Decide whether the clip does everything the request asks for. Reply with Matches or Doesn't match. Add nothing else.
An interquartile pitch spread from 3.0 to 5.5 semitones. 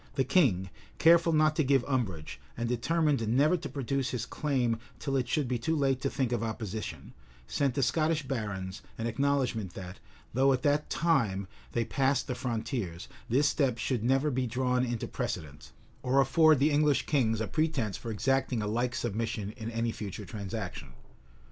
Matches